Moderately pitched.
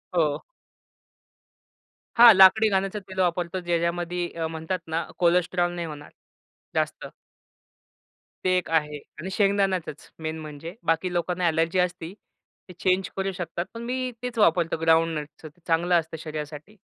Yes: medium, 175 Hz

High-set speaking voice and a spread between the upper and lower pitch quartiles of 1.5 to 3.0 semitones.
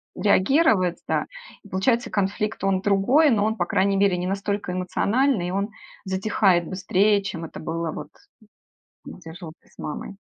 Yes: high, 195 Hz; narrow, 2.6 semitones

